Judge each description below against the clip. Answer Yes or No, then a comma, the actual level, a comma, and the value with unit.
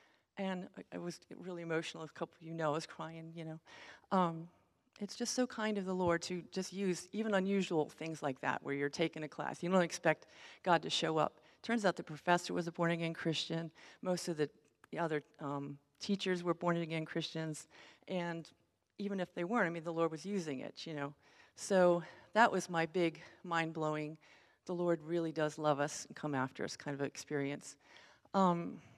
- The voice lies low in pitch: No, medium, 170 Hz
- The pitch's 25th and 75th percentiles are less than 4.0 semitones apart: Yes, average, 2.9 semitones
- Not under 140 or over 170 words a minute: No, average, 200 wpm